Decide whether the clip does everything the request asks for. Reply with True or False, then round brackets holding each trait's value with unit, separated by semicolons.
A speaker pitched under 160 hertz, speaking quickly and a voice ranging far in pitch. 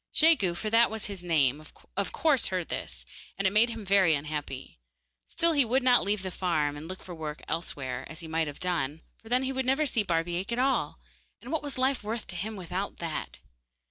False (190 Hz; 225 wpm; 6.5 semitones)